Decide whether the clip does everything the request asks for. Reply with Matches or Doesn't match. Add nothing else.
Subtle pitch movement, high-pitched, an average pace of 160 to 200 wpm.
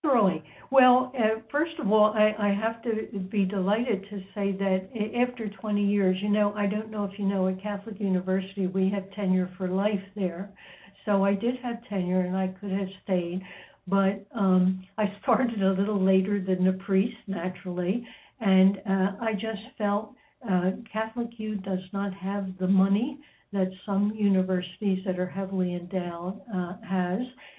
Matches